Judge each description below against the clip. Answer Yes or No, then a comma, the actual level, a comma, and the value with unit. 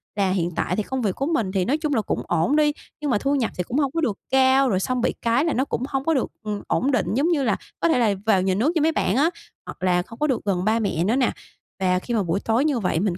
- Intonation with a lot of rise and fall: Yes, wide, 6.0 semitones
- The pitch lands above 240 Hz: No, high, 235 Hz